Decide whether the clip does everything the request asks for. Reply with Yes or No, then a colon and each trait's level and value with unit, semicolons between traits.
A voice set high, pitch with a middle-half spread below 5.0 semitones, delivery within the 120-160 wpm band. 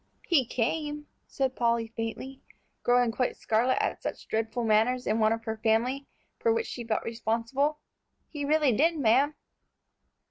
Yes: high, 245 Hz; average, 3.9 semitones; average, 150 wpm